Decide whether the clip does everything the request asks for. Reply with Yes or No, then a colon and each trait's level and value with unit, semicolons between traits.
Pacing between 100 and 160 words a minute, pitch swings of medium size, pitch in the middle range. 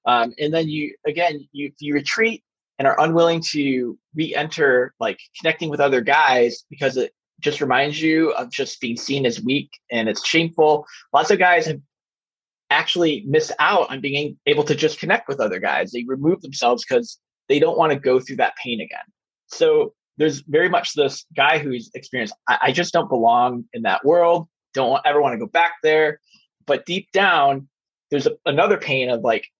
No: average, 190 wpm; average, 3.7 semitones; medium, 155 Hz